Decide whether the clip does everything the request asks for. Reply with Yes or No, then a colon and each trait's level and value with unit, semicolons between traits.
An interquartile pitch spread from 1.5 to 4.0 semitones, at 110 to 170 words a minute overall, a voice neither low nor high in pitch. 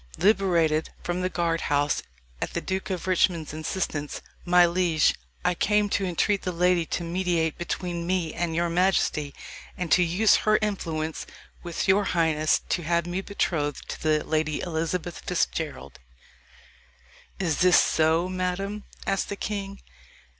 Yes: narrow, 2.5 semitones; average, 150 wpm; medium, 175 Hz